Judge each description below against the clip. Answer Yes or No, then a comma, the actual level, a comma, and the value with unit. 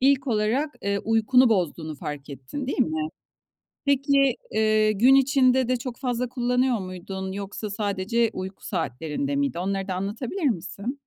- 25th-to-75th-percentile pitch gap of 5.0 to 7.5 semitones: Yes, average, 5.3 semitones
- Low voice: No, high, 220 Hz